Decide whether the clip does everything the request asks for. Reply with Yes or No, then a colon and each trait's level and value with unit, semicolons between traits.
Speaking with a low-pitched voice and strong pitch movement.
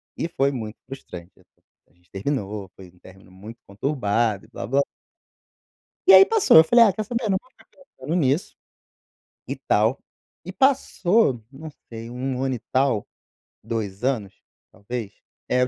Yes: low, 125 Hz; wide, 7.7 semitones